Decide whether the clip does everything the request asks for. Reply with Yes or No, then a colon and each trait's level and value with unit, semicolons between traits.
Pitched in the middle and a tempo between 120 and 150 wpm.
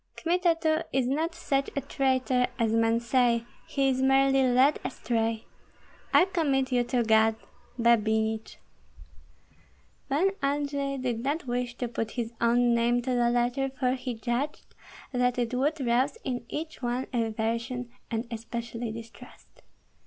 No: very high, 250 Hz; average, 145 wpm